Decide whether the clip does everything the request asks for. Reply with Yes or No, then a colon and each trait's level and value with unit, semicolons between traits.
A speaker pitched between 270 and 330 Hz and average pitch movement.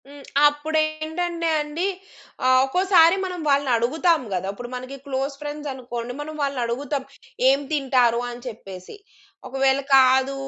Yes: very high, 275 Hz; average, 3.4 semitones